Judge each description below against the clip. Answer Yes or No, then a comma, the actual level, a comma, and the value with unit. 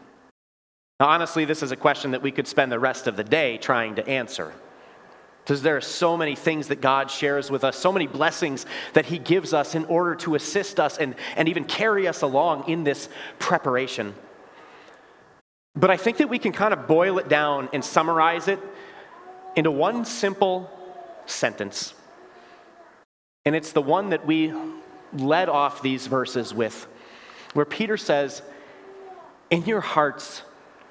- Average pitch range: No, wide, 5.8 semitones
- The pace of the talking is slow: No, average, 165 wpm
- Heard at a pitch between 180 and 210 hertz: No, medium, 160 Hz